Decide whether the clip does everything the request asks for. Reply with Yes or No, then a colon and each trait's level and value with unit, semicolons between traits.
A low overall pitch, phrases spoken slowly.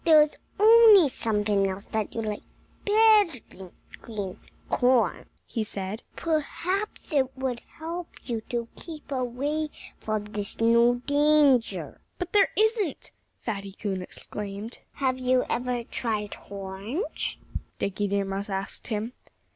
No: high, 245 Hz; slow, 130 wpm